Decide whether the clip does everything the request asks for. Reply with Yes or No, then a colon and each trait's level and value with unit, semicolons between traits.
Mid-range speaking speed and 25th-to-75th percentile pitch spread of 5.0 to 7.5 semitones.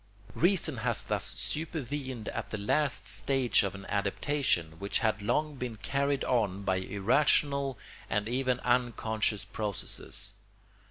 No: slow, 125 wpm; wide, 5.4 semitones